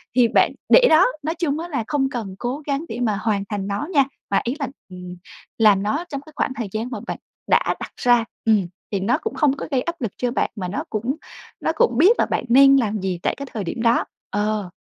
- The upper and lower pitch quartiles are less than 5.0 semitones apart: No, average, 5.3 semitones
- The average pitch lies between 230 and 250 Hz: Yes, high, 240 Hz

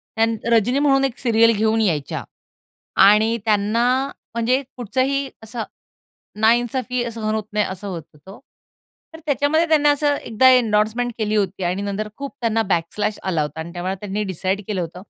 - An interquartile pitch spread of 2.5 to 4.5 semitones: Yes, average, 3.7 semitones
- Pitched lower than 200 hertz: No, high, 220 Hz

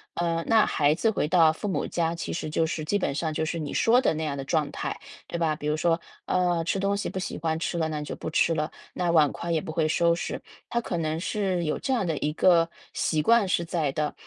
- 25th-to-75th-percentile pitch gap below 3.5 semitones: Yes, narrow, 2.4 semitones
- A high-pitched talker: No, medium, 165 Hz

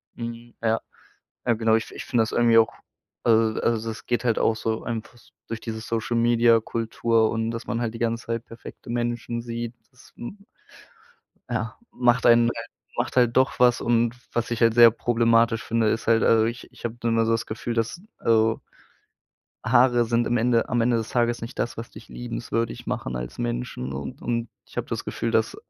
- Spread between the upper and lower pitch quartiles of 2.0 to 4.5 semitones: No, narrow, 0.9 semitones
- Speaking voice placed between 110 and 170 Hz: Yes, low, 115 Hz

